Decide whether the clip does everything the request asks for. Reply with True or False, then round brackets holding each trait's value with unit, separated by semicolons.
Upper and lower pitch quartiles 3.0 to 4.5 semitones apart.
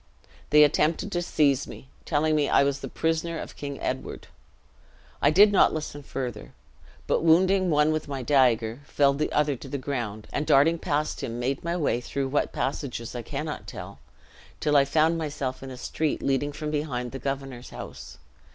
False (2.6 semitones)